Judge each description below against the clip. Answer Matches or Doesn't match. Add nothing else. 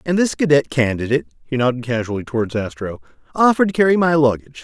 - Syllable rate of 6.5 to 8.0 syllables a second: Matches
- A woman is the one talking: Doesn't match